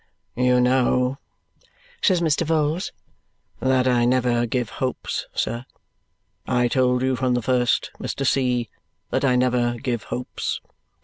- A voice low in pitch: Yes, low, 125 Hz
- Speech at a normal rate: No, slow, 130 wpm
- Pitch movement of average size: No, narrow, 1.2 semitones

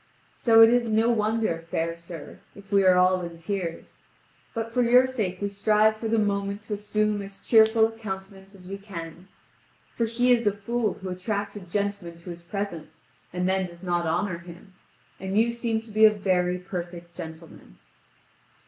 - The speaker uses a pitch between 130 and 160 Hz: No, high, 200 Hz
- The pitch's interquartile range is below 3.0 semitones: No, average, 3.5 semitones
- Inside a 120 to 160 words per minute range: No, average, 185 wpm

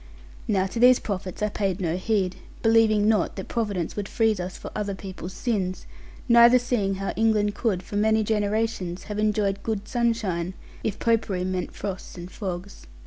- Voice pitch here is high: Yes, high, 205 Hz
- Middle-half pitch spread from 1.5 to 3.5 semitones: Yes, average, 2.9 semitones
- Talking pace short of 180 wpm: Yes, average, 170 wpm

